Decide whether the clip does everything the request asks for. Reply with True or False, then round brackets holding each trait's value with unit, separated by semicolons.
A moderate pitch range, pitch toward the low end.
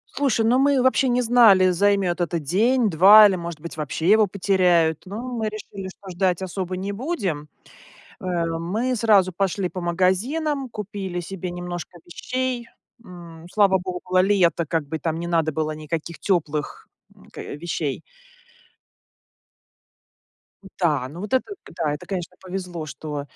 False (3.7 semitones; 185 Hz)